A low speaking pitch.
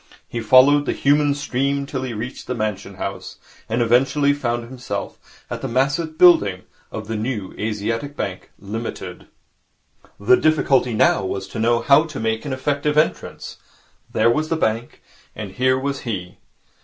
Yes: low, 125 Hz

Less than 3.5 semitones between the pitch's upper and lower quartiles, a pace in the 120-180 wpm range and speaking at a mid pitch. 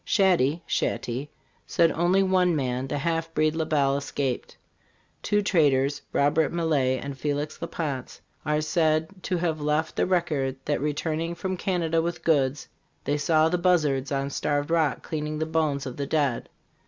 Yes: average, 2.9 semitones; average, 170 wpm; medium, 155 Hz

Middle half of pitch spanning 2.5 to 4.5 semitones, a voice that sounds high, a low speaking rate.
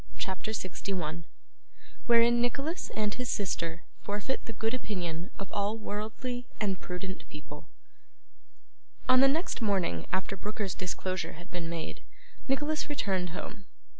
No: average, 4.9 semitones; high, 205 Hz; slow, 130 wpm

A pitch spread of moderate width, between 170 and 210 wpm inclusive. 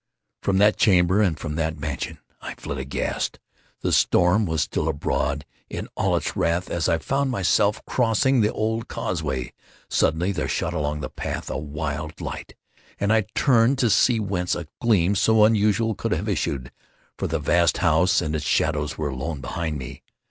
No: wide, 5.9 semitones; average, 175 wpm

